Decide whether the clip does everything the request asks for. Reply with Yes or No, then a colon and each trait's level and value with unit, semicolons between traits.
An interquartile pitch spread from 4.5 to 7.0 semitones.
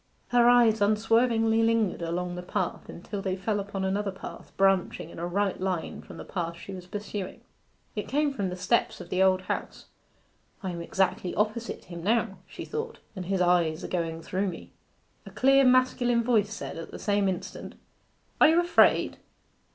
No: average, 3.9 semitones